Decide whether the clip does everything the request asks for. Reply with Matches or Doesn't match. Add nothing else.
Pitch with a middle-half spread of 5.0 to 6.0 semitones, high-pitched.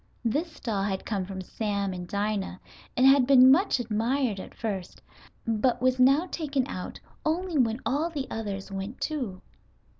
Matches